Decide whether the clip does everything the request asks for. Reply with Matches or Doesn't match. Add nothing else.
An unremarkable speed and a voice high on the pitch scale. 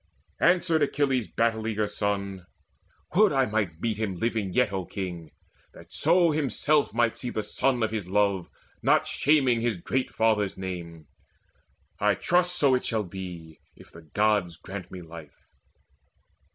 Doesn't match